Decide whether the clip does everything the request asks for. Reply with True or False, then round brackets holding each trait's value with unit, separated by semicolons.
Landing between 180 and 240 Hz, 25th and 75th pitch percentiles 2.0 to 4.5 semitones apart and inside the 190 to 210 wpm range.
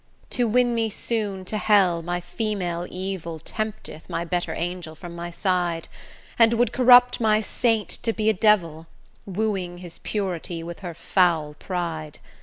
False (185 Hz; 4.1 semitones; 155 wpm)